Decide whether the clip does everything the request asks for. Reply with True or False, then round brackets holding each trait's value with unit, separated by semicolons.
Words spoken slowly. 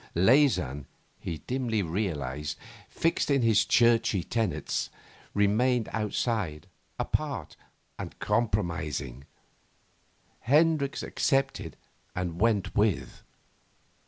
True (80 wpm)